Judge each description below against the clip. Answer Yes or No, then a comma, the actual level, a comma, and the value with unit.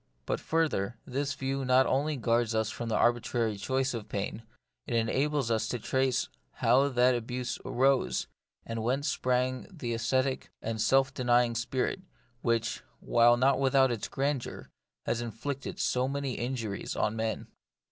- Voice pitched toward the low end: Yes, low, 125 Hz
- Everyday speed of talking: Yes, average, 150 wpm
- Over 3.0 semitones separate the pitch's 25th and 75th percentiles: No, narrow, 2.6 semitones